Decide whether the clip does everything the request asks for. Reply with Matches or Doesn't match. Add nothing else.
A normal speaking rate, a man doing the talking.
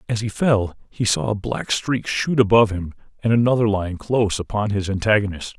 Matches